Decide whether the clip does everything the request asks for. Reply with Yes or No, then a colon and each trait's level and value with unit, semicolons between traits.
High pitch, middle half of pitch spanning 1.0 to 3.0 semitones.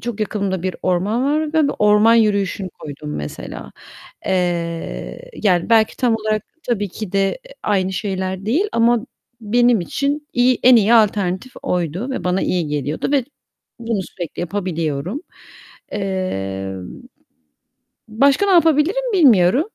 No: high, 205 Hz; average, 5.2 semitones